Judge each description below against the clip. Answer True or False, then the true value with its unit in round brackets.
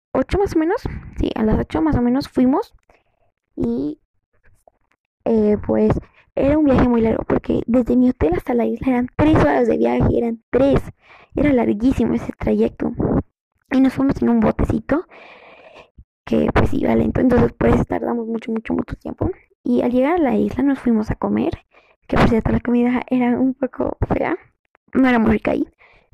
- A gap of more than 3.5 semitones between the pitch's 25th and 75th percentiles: False (3.0 semitones)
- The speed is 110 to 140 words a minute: False (185 wpm)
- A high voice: True (255 Hz)